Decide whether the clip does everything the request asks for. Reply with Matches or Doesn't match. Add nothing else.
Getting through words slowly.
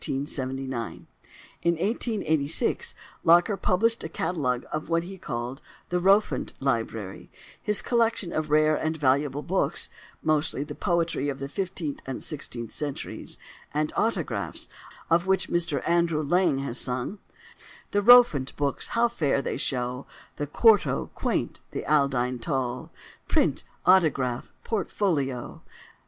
Matches